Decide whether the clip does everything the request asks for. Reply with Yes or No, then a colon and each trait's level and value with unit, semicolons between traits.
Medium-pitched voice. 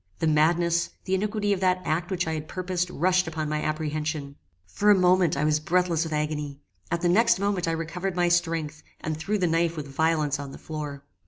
Yes: medium, 165 Hz